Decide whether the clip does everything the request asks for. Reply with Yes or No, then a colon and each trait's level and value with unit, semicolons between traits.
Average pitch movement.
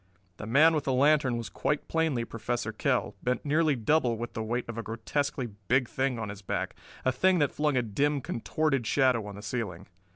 Yes: average, 4.2 semitones